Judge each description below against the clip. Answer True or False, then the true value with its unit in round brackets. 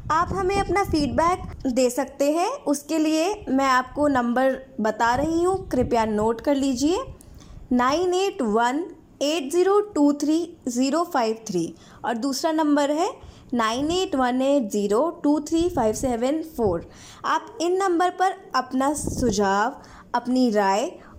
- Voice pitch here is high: True (280 Hz)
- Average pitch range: True (5.0 semitones)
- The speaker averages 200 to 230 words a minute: False (140 wpm)